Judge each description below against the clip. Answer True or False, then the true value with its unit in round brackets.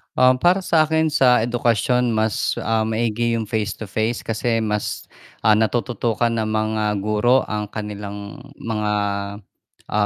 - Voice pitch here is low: True (110 Hz)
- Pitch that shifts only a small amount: True (2.2 semitones)